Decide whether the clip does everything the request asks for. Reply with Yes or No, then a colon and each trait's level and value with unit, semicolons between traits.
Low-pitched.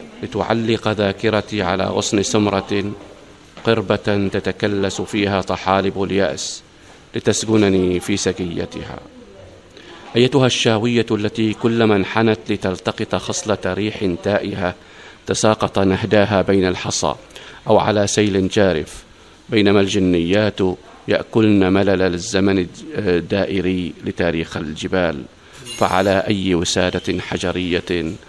Yes: low, 100 Hz